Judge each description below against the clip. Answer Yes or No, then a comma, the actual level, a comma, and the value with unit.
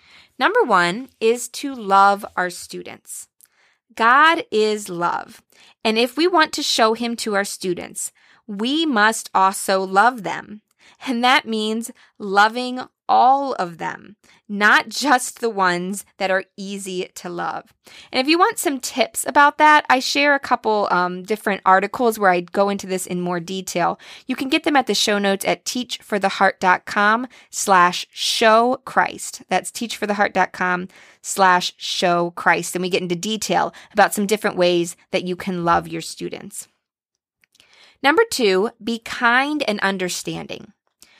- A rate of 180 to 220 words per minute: No, average, 145 wpm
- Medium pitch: No, high, 210 Hz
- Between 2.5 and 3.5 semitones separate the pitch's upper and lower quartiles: No, average, 4.9 semitones